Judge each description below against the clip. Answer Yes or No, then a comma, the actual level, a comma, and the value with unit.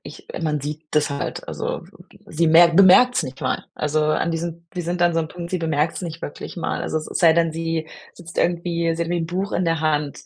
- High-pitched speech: No, medium, 165 Hz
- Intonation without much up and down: Yes, narrow, 1.8 semitones